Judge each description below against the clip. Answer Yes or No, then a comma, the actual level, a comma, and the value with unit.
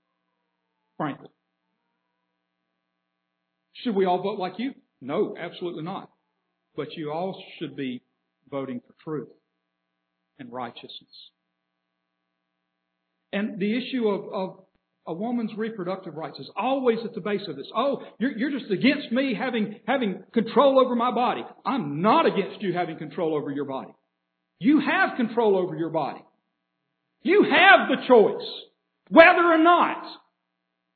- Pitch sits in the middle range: Yes, medium, 175 Hz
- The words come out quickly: No, slow, 135 wpm